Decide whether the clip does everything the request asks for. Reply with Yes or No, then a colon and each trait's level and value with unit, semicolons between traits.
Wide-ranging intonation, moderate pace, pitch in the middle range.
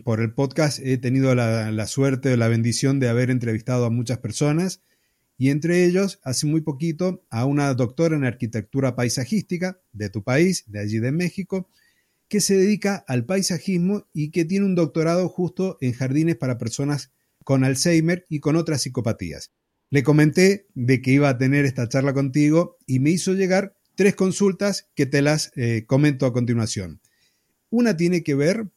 Yes: wide, 5.9 semitones; average, 175 wpm; medium, 145 Hz